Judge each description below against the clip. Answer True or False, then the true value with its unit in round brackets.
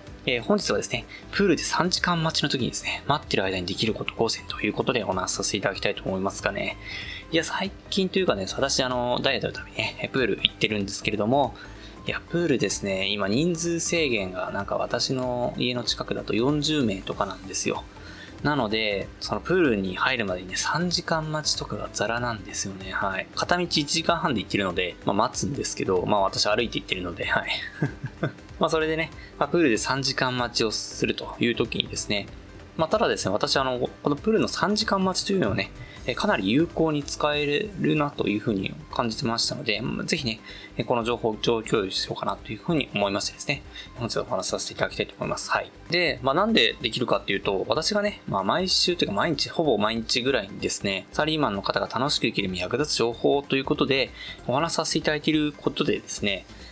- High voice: False (130 Hz)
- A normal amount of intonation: False (7.4 semitones)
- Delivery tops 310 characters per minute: True (435 characters per minute)